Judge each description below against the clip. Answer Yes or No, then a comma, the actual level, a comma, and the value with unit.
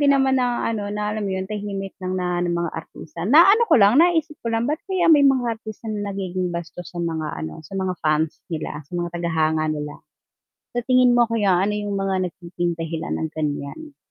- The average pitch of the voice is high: Yes, high, 195 Hz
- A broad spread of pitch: Yes, wide, 5.8 semitones